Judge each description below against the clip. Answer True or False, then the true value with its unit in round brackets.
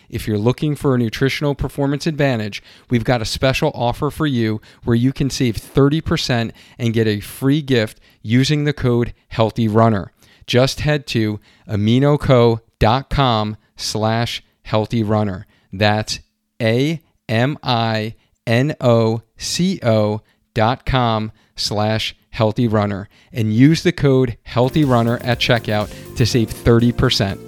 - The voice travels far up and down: False (3.4 semitones)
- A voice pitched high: False (115 Hz)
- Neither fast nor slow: False (110 wpm)